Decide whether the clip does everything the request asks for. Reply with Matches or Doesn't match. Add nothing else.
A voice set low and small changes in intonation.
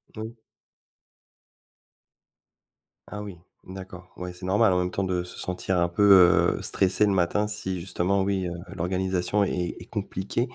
Matches